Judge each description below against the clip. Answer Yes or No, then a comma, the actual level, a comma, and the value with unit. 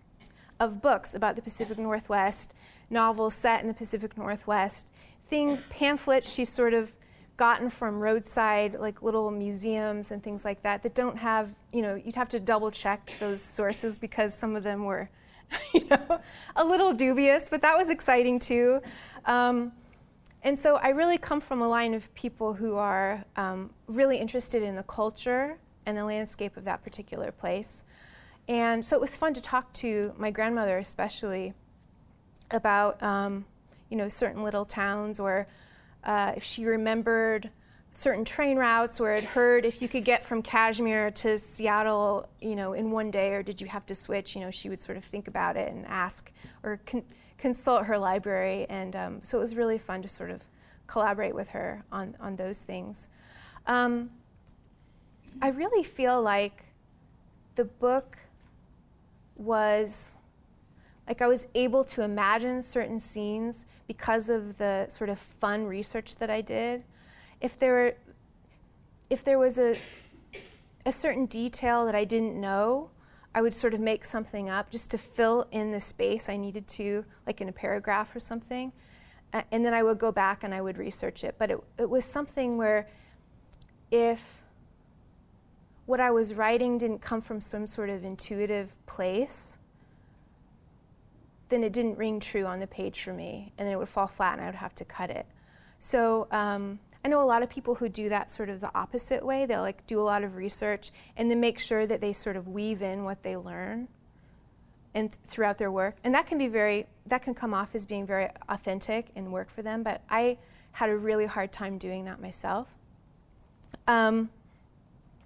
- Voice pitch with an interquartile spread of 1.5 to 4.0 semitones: Yes, average, 2.9 semitones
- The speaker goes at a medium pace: Yes, average, 180 wpm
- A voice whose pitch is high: Yes, high, 220 Hz